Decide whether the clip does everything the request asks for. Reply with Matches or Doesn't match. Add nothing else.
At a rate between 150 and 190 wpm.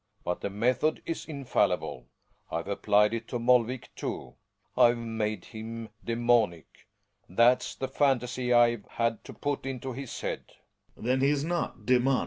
Matches